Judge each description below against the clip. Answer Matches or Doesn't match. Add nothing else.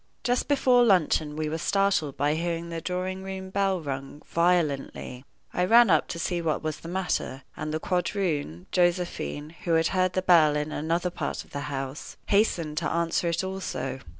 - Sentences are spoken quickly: Doesn't match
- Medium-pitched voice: Matches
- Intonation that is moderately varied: Matches